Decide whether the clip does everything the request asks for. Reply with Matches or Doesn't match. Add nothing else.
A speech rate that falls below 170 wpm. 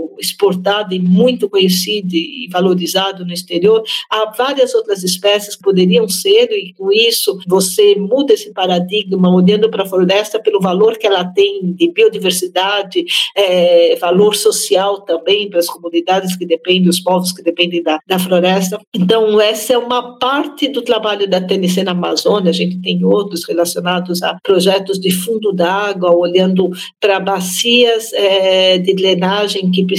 Matches